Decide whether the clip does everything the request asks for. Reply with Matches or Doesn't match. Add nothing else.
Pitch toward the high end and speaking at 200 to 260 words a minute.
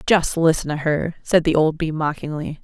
Doesn't match